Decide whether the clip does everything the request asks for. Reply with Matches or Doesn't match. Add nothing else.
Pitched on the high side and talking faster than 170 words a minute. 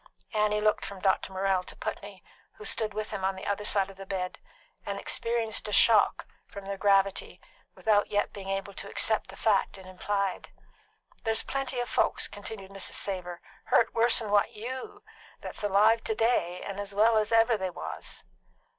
Matches